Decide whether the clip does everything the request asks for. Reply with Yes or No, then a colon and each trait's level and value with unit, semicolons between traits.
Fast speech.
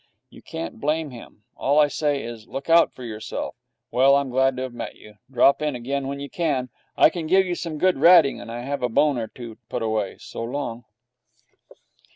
Yes: fast, 210 wpm